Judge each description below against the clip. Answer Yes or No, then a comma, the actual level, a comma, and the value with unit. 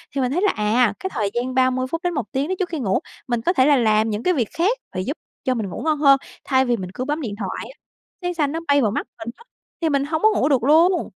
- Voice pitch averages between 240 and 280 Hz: Yes, very high, 265 Hz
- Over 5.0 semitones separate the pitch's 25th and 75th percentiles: Yes, wide, 5.4 semitones